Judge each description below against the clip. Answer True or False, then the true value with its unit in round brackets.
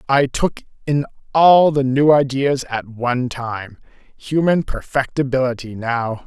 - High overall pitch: False (130 Hz)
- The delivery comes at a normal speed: False (115 wpm)